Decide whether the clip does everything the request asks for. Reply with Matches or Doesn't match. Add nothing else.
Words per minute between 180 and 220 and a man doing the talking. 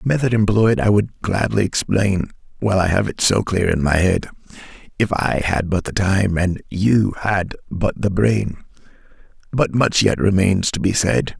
Matches